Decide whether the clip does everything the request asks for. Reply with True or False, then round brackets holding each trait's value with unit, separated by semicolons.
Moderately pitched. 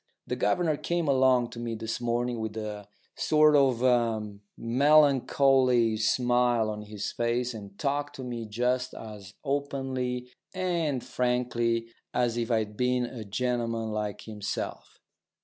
False (120 Hz)